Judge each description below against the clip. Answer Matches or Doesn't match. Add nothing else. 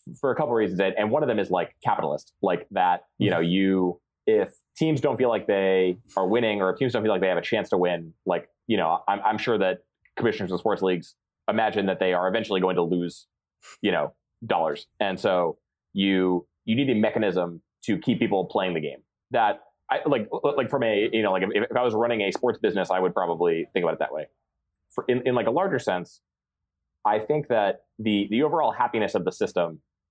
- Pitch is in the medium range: Doesn't match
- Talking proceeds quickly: Matches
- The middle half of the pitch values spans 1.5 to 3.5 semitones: Doesn't match